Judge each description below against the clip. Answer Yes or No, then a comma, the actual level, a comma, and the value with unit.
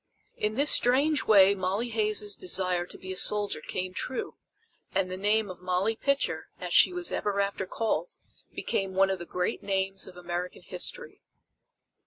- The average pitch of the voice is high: Yes, high, 195 Hz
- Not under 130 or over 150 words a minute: No, average, 170 wpm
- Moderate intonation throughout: Yes, average, 3.1 semitones